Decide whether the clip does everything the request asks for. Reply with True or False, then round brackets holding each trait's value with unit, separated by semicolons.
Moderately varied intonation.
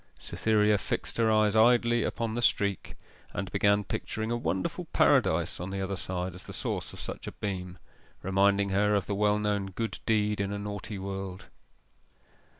False (1.8 semitones)